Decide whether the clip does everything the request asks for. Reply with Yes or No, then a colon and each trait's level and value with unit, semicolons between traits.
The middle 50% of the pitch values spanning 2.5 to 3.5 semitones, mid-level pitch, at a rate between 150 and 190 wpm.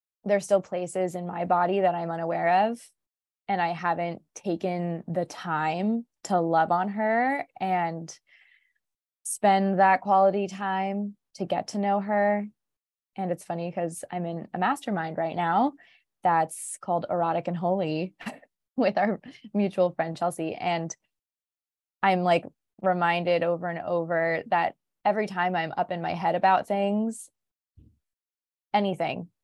No: average, 2.8 semitones; medium, 180 Hz; average, 140 wpm